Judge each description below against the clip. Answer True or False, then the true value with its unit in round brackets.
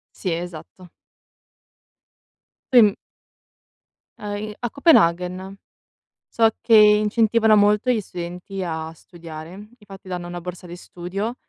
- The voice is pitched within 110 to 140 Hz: False (190 Hz)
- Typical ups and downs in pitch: True (3.4 semitones)